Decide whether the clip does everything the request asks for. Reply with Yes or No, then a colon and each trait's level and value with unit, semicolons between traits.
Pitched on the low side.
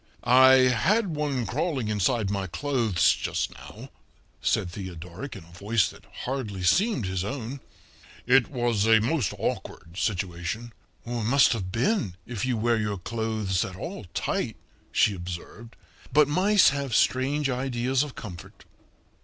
Yes: low, 115 Hz